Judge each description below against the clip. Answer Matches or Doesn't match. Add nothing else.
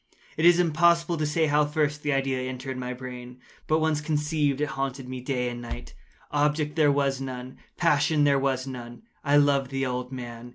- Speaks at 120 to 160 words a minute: Doesn't match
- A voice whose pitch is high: Doesn't match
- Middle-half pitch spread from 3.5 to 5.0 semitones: Doesn't match